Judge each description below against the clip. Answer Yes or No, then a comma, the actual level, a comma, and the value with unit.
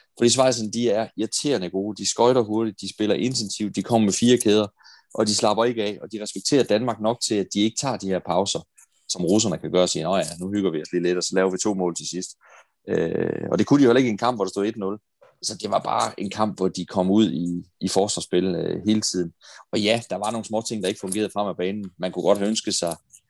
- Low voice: Yes, low, 105 Hz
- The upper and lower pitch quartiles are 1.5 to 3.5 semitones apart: Yes, average, 2.9 semitones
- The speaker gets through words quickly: Yes, fast, 275 wpm